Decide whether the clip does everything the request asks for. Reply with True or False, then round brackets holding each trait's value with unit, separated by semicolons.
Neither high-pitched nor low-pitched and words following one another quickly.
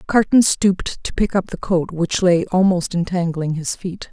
False (180 Hz; 190 wpm)